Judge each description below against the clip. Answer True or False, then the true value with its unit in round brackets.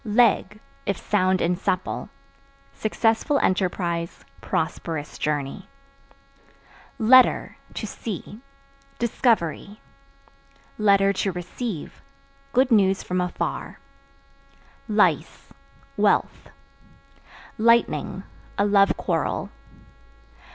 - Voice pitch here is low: False (200 Hz)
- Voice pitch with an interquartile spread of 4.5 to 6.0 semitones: False (3.7 semitones)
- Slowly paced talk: True (75 wpm)